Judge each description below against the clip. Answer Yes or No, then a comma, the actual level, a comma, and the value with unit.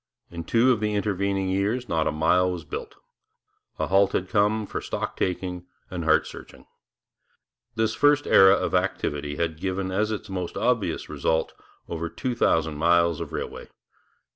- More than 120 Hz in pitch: No, very low, 95 Hz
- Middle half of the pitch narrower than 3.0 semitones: No, average, 3.8 semitones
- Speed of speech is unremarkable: Yes, average, 165 wpm